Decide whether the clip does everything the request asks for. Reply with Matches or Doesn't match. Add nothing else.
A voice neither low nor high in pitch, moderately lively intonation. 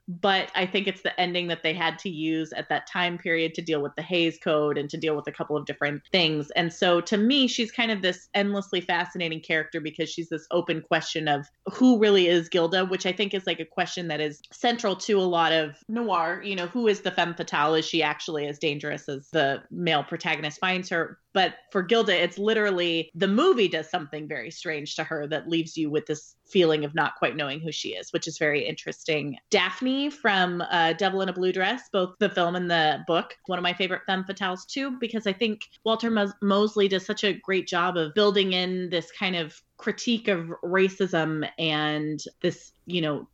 Matches